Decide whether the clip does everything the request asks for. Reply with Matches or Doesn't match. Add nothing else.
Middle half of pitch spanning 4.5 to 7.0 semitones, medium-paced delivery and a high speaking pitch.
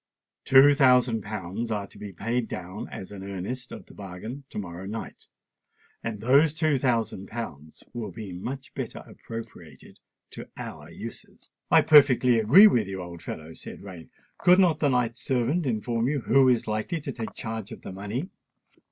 Doesn't match